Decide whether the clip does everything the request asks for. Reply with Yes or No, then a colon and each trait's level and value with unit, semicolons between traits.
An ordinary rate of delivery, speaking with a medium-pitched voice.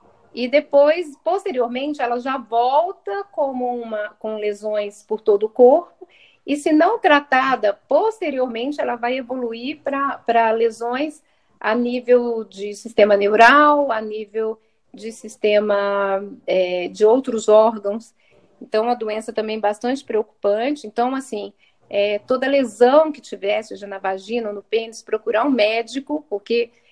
No: average, 135 wpm; high, 235 Hz